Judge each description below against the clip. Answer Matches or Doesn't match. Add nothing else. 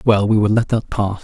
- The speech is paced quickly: Matches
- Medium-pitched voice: Doesn't match